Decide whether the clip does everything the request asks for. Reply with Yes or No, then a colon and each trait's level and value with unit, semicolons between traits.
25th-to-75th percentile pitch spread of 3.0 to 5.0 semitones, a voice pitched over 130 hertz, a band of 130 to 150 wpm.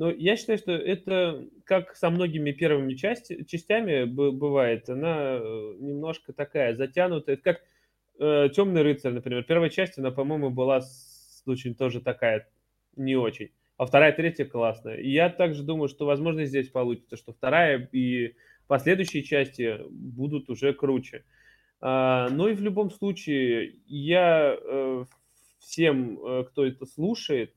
Yes: average, 4.6 semitones; medium, 140 Hz; average, 140 wpm